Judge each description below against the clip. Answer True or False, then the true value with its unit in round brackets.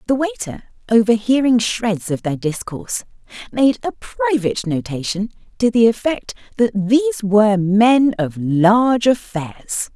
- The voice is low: False (220 Hz)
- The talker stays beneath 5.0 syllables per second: True (4.6 syllables/s)